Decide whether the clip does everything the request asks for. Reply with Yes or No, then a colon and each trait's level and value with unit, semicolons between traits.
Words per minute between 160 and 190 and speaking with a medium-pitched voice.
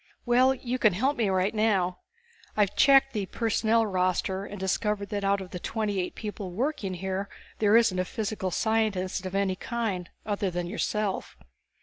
No: average, 170 wpm; high, 205 Hz